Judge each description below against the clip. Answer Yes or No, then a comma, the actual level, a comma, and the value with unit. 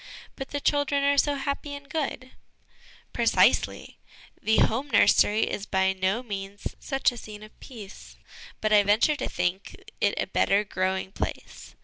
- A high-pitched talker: Yes, high, 220 Hz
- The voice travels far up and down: Yes, wide, 6.0 semitones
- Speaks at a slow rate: No, average, 165 wpm